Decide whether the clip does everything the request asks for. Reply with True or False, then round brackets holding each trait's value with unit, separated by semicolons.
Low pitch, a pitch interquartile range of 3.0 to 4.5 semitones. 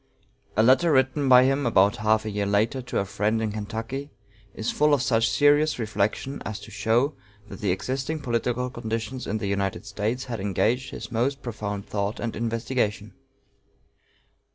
True (115 Hz; 3.9 semitones)